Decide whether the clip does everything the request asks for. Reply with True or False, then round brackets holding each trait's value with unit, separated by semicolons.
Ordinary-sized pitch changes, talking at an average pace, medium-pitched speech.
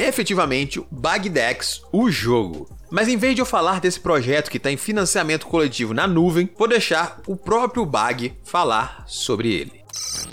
False (6.7 semitones; 175 wpm; 180 Hz)